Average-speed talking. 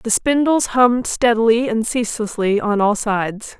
Yes: average, 150 wpm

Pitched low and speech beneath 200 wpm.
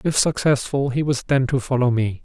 No: low, 130 Hz; fast, 215 wpm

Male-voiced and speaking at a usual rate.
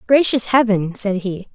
No: female; average, 155 wpm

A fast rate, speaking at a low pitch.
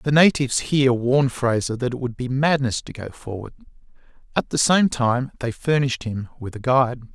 No: average, 195 wpm; low, 130 Hz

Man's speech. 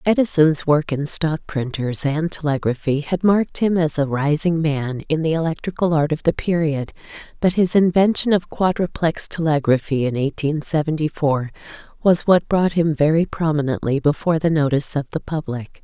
No: female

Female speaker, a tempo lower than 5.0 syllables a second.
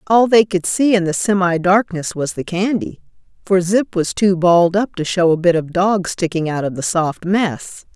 Yes: female; 4.7 syllables/s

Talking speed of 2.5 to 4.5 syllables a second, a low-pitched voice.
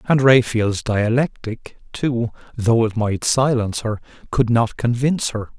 Yes: 4.3 syllables/s; low, 115 Hz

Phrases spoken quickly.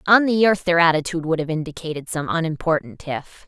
No: average, 190 wpm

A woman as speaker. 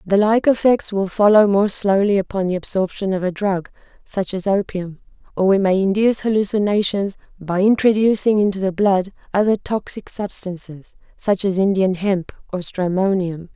Yes: female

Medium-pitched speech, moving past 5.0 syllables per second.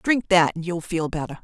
Yes: medium, 175 Hz; 5.4 syllables/s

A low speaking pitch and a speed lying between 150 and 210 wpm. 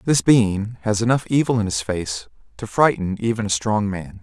Yes: low, 110 Hz; average, 200 wpm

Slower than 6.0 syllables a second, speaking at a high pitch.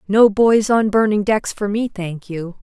Yes: 4.1 syllables/s; high, 205 Hz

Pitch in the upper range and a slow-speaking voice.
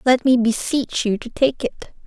No: high, 245 Hz; fast, 205 wpm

